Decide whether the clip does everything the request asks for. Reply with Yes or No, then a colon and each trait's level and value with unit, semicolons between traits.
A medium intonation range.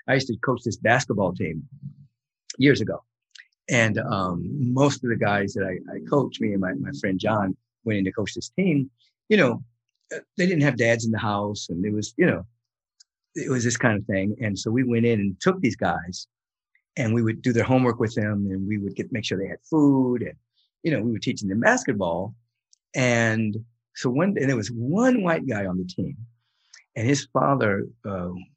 Yes: average, 4.0 semitones